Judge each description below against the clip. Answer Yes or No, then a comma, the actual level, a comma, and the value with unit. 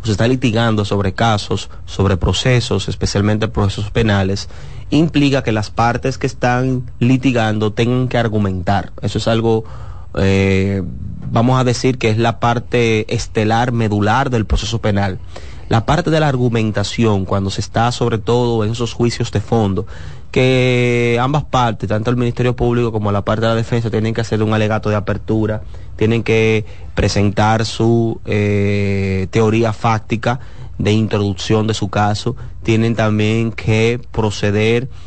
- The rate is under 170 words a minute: Yes, average, 150 wpm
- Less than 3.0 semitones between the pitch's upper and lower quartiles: Yes, narrow, 2.6 semitones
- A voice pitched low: Yes, low, 110 Hz